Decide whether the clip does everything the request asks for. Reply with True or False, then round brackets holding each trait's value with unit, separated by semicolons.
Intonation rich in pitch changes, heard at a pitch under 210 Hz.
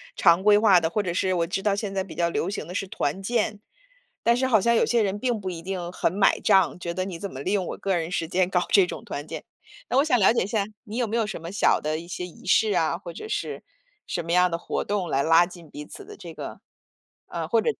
False (3.5 semitones; 190 Hz)